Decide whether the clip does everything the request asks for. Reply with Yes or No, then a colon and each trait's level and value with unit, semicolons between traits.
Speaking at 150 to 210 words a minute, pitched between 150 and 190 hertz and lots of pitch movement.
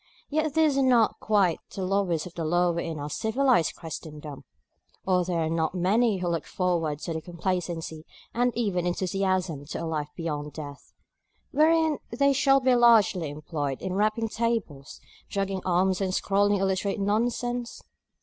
Yes: average, 155 wpm; medium, 185 Hz; wide, 5.7 semitones